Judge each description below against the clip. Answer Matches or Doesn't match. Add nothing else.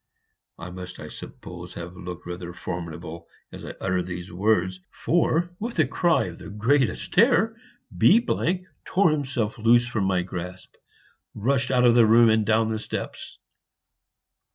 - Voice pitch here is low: Matches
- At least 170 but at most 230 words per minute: Doesn't match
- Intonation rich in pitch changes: Matches